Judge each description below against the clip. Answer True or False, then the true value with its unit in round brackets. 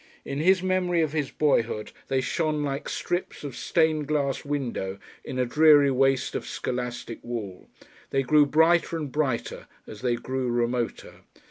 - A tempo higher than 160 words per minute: False (155 wpm)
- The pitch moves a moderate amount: True (3.9 semitones)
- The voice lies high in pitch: False (140 Hz)